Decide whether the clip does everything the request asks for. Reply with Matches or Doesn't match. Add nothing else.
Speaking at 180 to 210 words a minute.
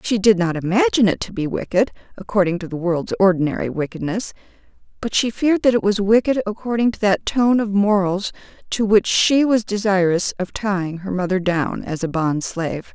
Matches